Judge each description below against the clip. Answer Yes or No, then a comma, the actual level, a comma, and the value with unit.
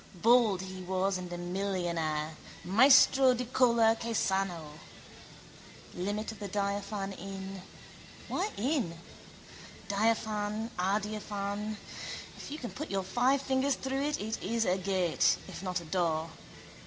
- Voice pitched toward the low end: No, high, 200 Hz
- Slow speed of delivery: Yes, slow, 130 wpm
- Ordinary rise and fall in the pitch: Yes, average, 3.9 semitones